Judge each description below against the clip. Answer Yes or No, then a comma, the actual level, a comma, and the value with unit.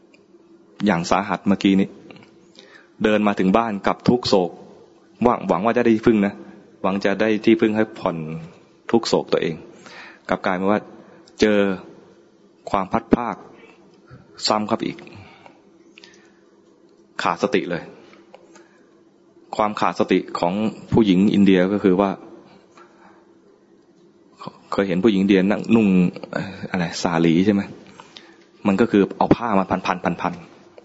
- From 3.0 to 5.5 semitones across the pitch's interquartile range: No, narrow, 2.4 semitones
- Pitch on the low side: Yes, low, 100 Hz